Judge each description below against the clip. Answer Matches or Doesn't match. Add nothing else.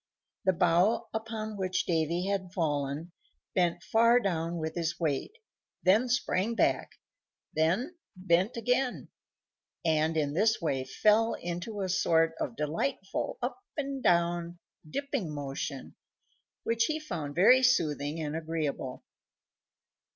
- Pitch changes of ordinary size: Doesn't match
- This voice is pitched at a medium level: Matches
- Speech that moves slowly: Matches